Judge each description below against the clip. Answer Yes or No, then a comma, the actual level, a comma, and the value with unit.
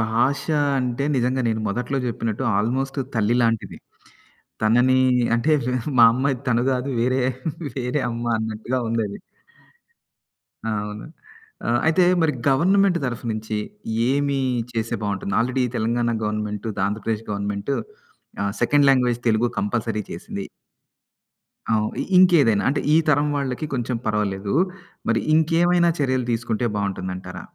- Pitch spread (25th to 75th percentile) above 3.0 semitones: Yes, average, 3.7 semitones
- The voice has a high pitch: No, low, 120 Hz